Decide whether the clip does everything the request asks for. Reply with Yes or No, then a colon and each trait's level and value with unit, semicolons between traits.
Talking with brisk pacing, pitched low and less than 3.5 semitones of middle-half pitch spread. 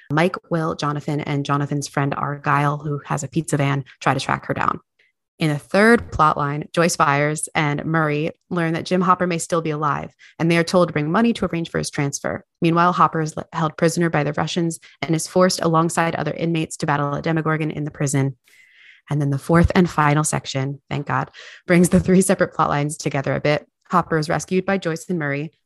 No: fast, 215 wpm; medium, 160 Hz; narrow, 2.6 semitones